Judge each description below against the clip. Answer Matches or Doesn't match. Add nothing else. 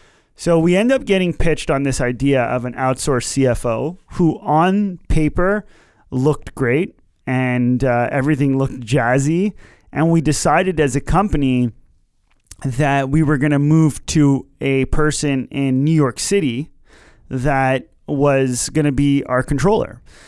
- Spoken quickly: Doesn't match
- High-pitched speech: Doesn't match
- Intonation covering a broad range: Doesn't match